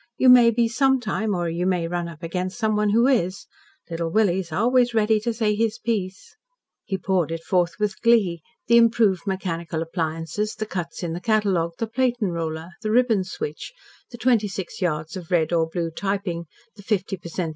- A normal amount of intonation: Yes, average, 4.6 semitones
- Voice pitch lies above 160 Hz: Yes, high, 190 Hz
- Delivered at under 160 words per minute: No, average, 190 wpm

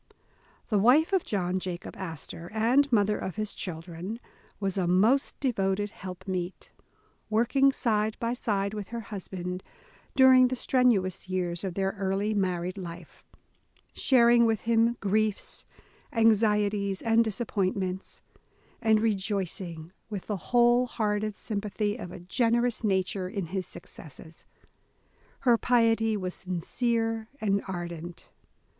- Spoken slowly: Yes, slow, 125 wpm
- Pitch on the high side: Yes, high, 205 Hz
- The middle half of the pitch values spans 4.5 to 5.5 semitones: No, average, 3.6 semitones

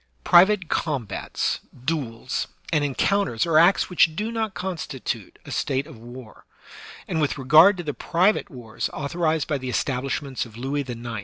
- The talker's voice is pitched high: No, medium, 145 Hz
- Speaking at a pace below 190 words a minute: Yes, average, 155 wpm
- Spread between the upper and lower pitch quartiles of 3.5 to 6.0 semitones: Yes, average, 5.2 semitones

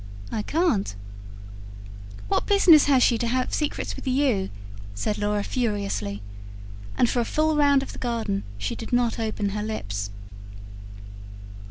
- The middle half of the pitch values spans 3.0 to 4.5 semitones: No, average, 5.0 semitones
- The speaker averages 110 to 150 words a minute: Yes, average, 145 wpm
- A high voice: Yes, high, 230 Hz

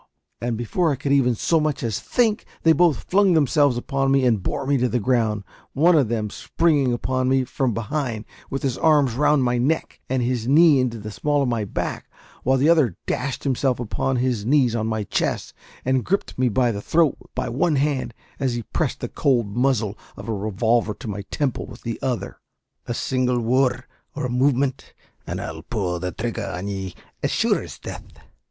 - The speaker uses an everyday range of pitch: Yes, average, 3.5 semitones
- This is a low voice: Yes, low, 125 Hz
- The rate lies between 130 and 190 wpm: No, average, 200 wpm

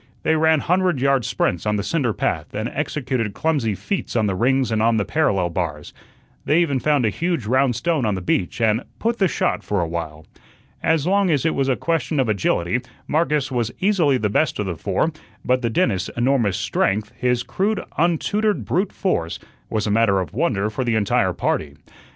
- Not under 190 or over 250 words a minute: Yes, average, 200 wpm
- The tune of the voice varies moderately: No, wide, 7.3 semitones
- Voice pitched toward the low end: Yes, low, 125 Hz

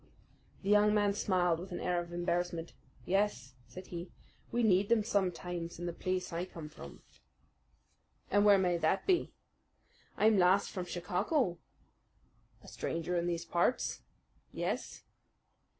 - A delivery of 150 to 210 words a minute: No, average, 140 wpm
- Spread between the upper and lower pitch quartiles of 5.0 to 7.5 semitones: No, average, 2.8 semitones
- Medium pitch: Yes, medium, 180 Hz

